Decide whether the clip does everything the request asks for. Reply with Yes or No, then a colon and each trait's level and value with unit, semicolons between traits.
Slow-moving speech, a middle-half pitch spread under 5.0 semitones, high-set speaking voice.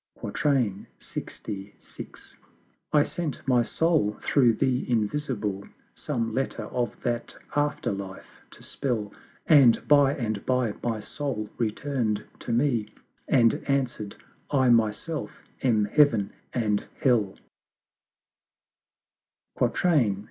No: slow, 100 wpm; average, 4.6 semitones; low, 120 Hz